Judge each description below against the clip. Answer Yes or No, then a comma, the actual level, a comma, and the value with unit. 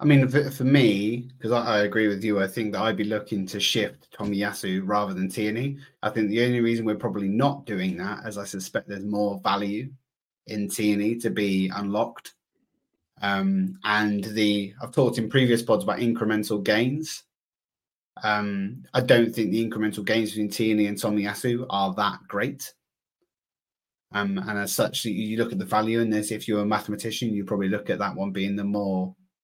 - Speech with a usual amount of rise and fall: No, narrow, 2.3 semitones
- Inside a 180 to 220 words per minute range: Yes, average, 190 wpm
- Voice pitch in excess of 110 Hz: No, low, 105 Hz